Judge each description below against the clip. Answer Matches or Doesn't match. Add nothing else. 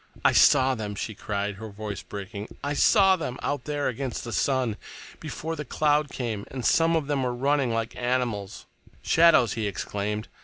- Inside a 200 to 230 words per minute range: Doesn't match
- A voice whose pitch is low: Matches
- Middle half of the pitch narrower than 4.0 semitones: Doesn't match